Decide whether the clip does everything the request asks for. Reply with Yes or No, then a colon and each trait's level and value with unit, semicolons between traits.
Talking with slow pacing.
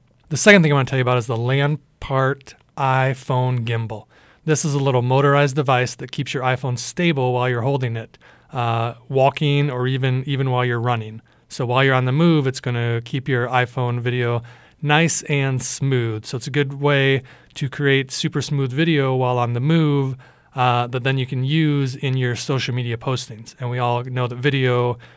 No: average, 200 wpm